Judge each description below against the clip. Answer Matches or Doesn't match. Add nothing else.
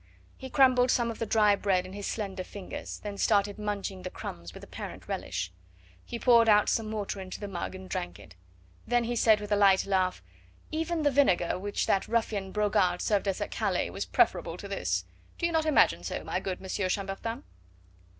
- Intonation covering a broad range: Doesn't match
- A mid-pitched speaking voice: Doesn't match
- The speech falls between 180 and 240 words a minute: Matches